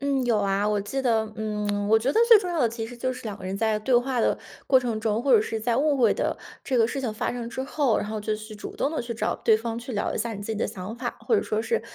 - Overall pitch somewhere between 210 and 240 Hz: Yes, high, 230 Hz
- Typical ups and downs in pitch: Yes, average, 3.1 semitones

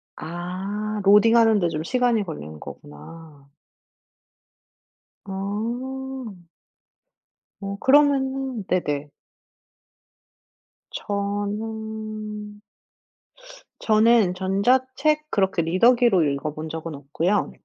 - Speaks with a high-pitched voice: Yes, high, 205 Hz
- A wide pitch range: No, average, 5.0 semitones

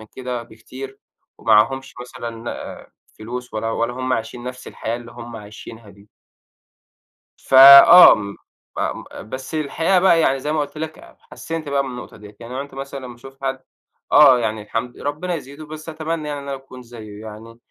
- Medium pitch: No, low, 130 Hz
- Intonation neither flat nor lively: Yes, average, 3.5 semitones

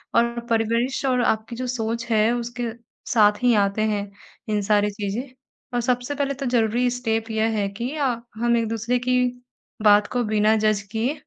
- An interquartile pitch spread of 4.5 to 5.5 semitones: No, narrow, 2.4 semitones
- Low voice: No, high, 230 Hz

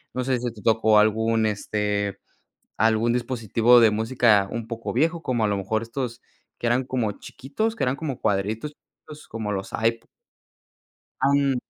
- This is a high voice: No, low, 115 Hz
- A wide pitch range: No, average, 2.9 semitones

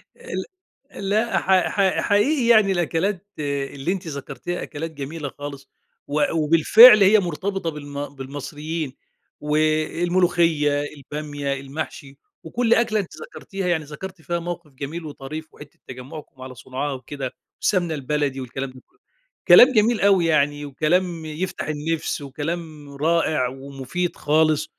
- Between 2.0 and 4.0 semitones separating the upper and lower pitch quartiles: Yes, average, 3.7 semitones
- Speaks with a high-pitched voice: No, medium, 155 Hz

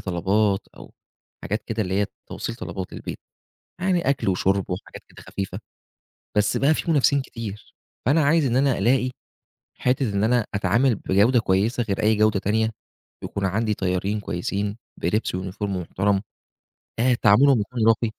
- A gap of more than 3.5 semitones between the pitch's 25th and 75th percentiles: Yes, average, 4.2 semitones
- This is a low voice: Yes, low, 105 Hz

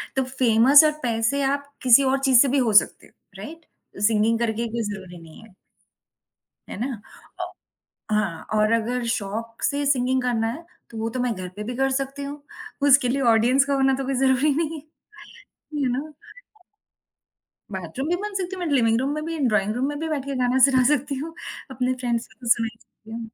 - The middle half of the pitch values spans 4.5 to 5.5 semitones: No, average, 3.6 semitones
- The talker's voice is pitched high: Yes, very high, 255 Hz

